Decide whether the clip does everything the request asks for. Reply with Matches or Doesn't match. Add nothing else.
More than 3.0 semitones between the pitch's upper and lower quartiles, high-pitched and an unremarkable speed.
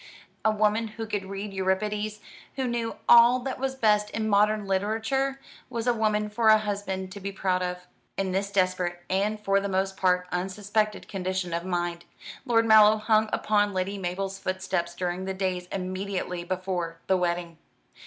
Doesn't match